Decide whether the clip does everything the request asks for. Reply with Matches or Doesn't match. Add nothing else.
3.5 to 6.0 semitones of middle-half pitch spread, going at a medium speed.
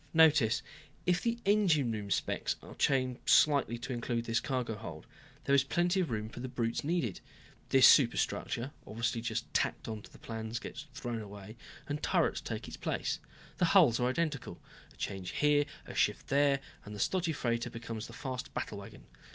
Matches